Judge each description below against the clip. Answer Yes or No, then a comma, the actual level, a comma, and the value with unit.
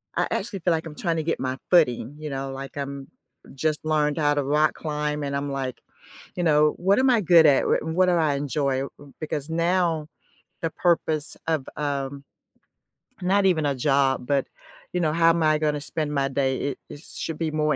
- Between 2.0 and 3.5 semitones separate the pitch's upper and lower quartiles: Yes, average, 2.7 semitones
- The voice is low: No, medium, 150 Hz